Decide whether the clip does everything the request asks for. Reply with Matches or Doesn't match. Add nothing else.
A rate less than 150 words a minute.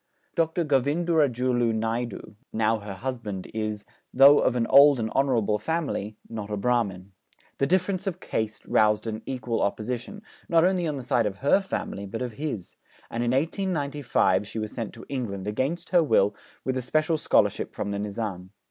Doesn't match